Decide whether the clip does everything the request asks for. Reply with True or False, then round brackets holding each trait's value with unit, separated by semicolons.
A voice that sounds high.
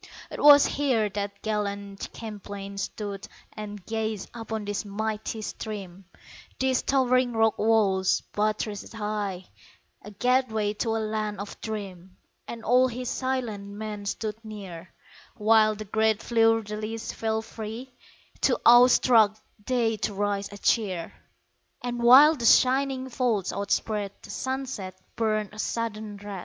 True (215 Hz)